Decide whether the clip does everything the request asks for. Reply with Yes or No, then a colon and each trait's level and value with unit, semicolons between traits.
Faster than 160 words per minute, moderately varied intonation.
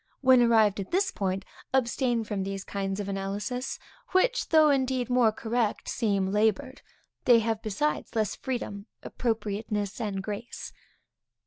No: slow, 135 wpm; average, 3.8 semitones